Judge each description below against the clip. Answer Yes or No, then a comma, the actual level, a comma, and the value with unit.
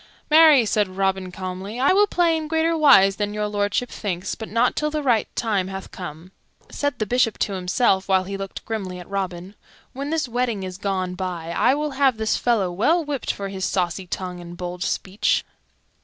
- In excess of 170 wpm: Yes, average, 200 wpm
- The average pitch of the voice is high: Yes, high, 200 Hz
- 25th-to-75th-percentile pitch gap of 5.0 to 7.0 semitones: Yes, average, 5.3 semitones